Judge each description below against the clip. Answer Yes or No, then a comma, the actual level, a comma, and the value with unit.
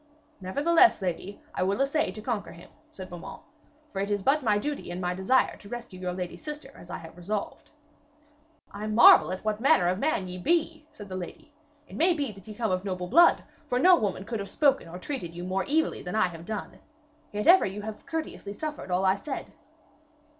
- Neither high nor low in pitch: No, high, 205 Hz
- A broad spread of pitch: Yes, wide, 7.2 semitones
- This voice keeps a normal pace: No, fast, 210 wpm